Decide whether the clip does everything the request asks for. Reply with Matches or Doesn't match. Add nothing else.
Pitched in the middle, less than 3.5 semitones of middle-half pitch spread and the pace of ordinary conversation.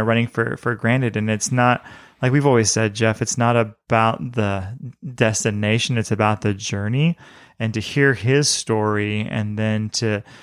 Doesn't match